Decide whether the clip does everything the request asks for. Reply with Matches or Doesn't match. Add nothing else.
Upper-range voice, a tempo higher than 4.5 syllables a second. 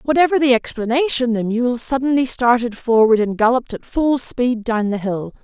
Matches